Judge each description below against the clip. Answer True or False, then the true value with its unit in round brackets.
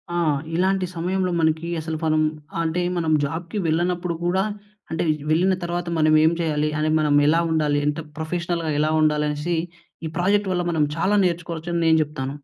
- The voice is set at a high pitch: False (165 Hz)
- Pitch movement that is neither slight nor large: False (2.1 semitones)